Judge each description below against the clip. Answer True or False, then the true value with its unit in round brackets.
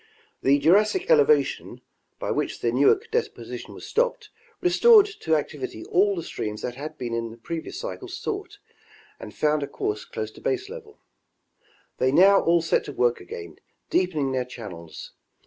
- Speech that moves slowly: False (155 wpm)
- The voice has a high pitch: False (170 Hz)